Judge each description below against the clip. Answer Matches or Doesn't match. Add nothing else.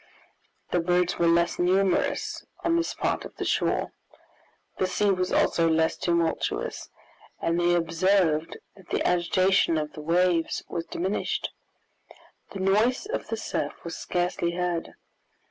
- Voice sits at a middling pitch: Matches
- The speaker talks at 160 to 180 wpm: Doesn't match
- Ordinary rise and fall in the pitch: Doesn't match